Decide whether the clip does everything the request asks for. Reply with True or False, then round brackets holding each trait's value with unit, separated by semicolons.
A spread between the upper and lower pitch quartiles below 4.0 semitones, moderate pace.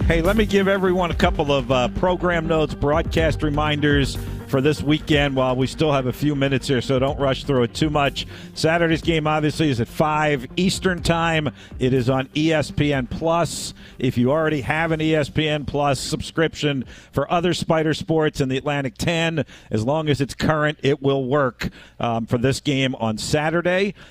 True (3.3 semitones; 185 wpm)